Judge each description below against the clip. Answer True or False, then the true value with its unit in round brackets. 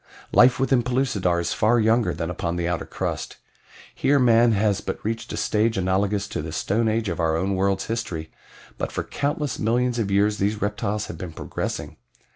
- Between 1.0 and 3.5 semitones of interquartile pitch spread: False (3.9 semitones)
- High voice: False (105 Hz)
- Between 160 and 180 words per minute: False (190 wpm)